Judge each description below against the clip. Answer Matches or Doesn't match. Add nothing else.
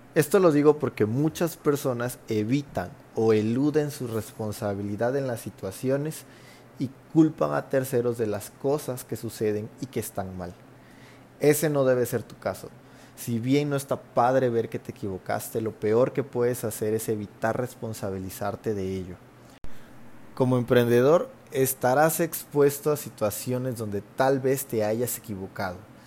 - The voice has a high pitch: Doesn't match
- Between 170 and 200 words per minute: Doesn't match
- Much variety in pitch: Doesn't match